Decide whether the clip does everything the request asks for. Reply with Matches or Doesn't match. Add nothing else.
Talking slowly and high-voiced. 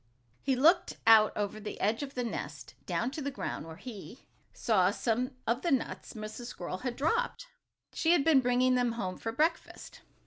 Doesn't match